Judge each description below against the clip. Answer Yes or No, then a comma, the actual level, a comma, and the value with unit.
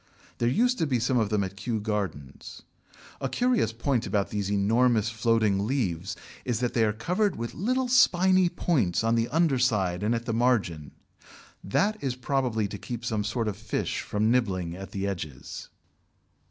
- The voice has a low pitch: Yes, low, 115 Hz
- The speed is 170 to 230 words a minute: Yes, average, 180 wpm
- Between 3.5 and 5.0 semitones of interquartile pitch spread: Yes, average, 4.1 semitones